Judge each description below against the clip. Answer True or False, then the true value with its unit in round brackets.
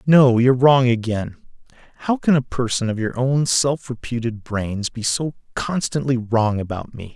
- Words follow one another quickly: False (160 wpm)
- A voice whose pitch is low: True (125 Hz)